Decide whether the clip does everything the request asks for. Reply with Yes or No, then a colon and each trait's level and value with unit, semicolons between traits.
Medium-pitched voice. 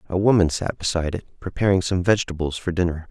No: very low, 90 Hz